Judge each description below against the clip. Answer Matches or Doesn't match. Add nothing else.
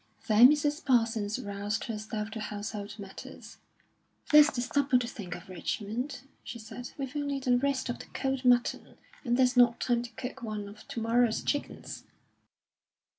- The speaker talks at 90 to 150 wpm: Doesn't match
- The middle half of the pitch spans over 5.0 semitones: Doesn't match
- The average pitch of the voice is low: Doesn't match